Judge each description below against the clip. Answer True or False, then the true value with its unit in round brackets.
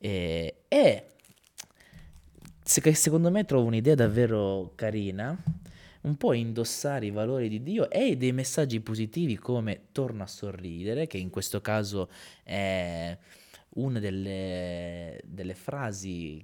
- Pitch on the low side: True (105 Hz)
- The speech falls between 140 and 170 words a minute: False (120 wpm)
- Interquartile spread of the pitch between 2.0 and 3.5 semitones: False (5.2 semitones)